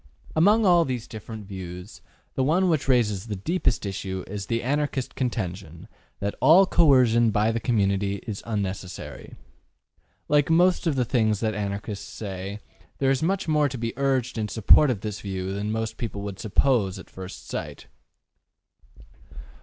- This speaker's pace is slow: No, average, 160 wpm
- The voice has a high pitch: No, low, 110 Hz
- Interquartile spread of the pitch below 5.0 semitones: No, average, 5.3 semitones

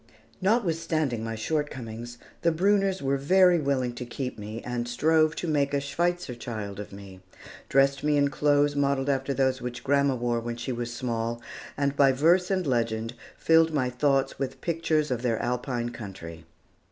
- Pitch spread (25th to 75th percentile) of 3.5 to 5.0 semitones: Yes, average, 4.1 semitones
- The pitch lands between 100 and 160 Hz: Yes, low, 135 Hz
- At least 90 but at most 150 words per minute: No, average, 170 wpm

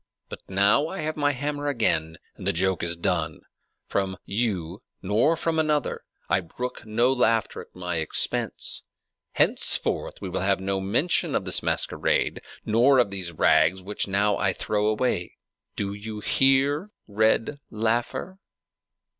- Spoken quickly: No, average, 145 wpm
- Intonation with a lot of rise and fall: Yes, wide, 5.8 semitones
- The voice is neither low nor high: No, low, 105 Hz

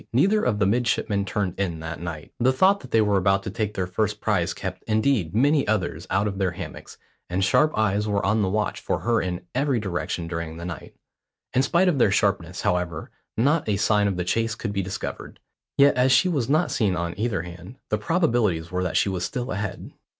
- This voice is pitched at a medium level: No, low, 105 Hz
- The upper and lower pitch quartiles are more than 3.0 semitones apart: Yes, average, 5.1 semitones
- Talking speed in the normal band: No, fast, 220 wpm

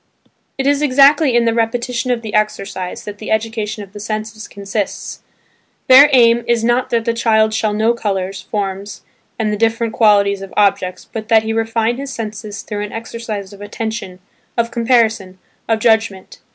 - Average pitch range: No, narrow, 2.1 semitones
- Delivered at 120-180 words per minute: Yes, average, 175 wpm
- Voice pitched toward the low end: No, high, 220 Hz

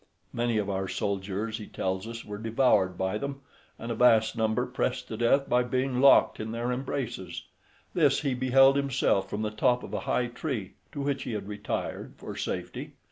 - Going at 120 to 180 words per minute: No, average, 190 wpm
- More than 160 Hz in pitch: No, low, 115 Hz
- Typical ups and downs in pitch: Yes, average, 3.7 semitones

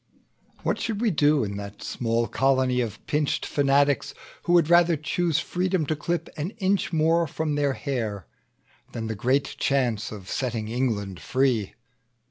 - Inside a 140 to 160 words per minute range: Yes, average, 155 wpm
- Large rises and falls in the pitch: Yes, wide, 5.7 semitones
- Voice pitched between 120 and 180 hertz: Yes, medium, 140 Hz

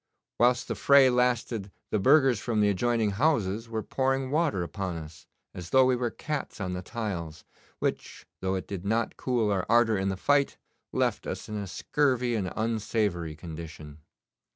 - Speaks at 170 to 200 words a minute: Yes, average, 175 wpm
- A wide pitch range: No, average, 5.0 semitones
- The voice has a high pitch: No, low, 110 Hz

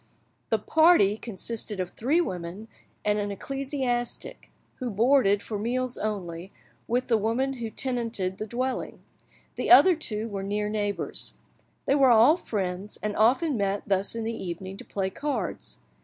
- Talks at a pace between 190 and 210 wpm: No, average, 155 wpm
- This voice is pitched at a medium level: No, high, 220 Hz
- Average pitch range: Yes, average, 4.2 semitones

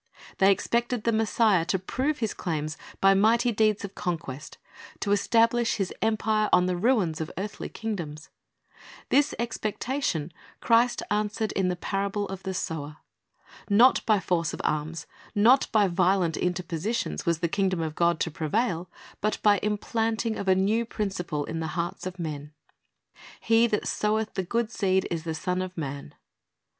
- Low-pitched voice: No, high, 195 Hz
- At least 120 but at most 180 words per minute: Yes, average, 165 wpm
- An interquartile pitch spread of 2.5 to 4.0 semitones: No, average, 4.5 semitones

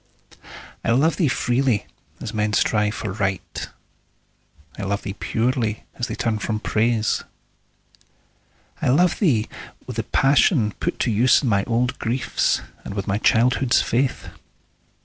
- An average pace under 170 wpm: Yes, average, 145 wpm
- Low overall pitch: Yes, low, 115 Hz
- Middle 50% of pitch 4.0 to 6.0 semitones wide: No, average, 3.1 semitones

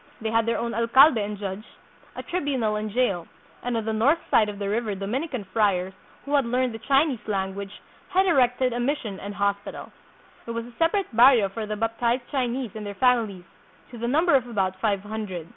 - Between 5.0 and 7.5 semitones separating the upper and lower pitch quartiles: No, average, 3.7 semitones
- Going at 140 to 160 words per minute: No, fast, 205 wpm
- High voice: Yes, high, 230 Hz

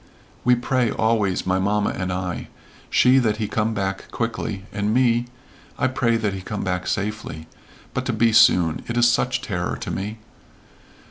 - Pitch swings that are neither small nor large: Yes, average, 3.4 semitones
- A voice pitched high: No, low, 105 Hz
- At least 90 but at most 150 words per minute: No, average, 175 wpm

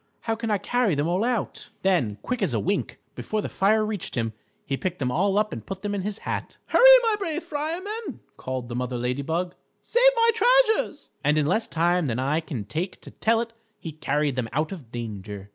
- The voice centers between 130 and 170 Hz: No, medium, 180 Hz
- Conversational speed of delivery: No, fast, 220 wpm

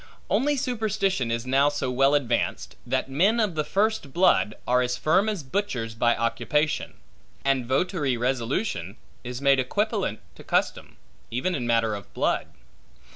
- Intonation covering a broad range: Yes, wide, 8.0 semitones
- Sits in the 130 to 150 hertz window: Yes, low, 135 Hz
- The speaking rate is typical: Yes, average, 150 wpm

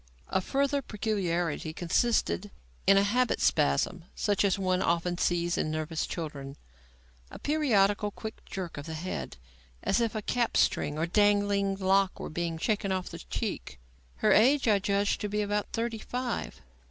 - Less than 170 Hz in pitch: No, high, 195 Hz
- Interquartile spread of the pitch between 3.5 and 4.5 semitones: Yes, average, 3.9 semitones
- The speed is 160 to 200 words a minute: Yes, average, 165 wpm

